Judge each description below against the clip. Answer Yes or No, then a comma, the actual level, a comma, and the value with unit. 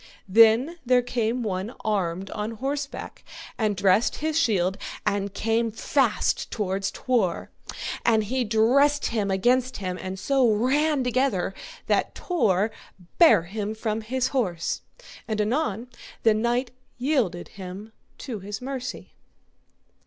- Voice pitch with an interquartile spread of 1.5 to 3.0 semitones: No, average, 4.2 semitones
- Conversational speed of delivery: No, slow, 125 wpm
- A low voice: No, high, 225 Hz